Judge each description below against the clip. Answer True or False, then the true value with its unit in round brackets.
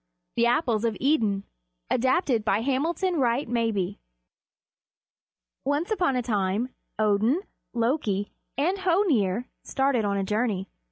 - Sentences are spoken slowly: True (115 wpm)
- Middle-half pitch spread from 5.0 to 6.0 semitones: True (5.3 semitones)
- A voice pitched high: True (235 Hz)